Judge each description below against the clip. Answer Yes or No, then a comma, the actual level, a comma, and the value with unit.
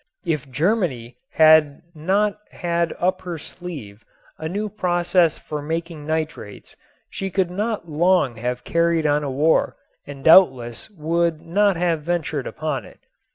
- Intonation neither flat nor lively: Yes, average, 3.2 semitones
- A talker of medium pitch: Yes, medium, 165 Hz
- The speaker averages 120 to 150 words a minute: Yes, average, 140 wpm